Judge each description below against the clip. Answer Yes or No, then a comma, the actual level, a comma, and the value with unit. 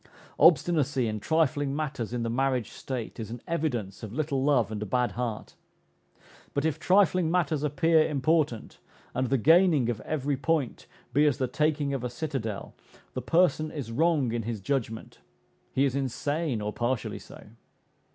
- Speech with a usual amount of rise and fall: Yes, average, 4.6 semitones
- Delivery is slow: No, average, 165 wpm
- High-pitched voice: No, low, 135 Hz